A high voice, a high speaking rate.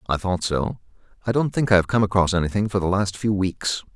No: low, 100 Hz; fast, 240 wpm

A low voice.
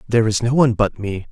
Yes: low, 110 Hz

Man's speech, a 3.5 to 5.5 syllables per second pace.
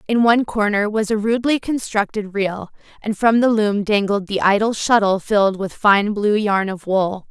No: female; 4.8 syllables/s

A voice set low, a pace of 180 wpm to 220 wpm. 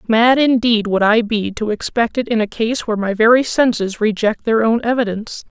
No: high, 225 Hz; fast, 205 wpm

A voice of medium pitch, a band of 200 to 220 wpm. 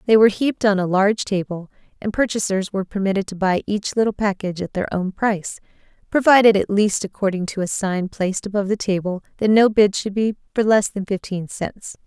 No: high, 200 Hz; fast, 205 wpm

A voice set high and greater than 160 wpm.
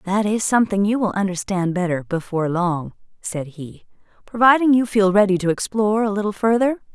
Yes: high, 200 Hz; average, 175 wpm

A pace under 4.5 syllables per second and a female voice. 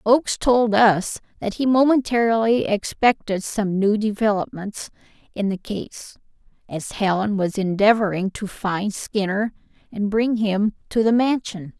Yes: 4.2 syllables/s; female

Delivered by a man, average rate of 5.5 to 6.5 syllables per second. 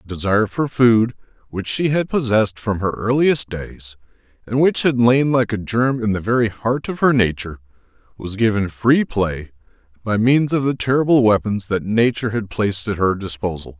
No: male; 5.1 syllables/s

